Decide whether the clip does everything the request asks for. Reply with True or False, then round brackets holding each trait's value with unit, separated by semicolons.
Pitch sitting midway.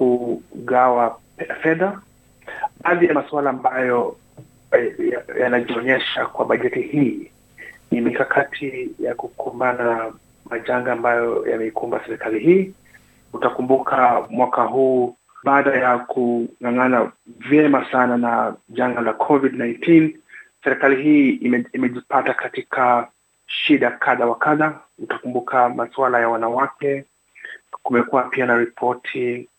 False (125 Hz)